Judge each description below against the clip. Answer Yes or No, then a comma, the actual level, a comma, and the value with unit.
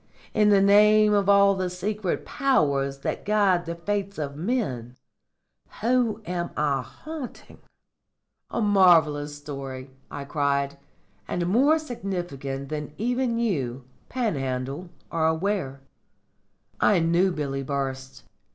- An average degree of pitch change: No, wide, 6.8 semitones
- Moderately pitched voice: Yes, medium, 175 Hz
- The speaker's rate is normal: No, slow, 115 wpm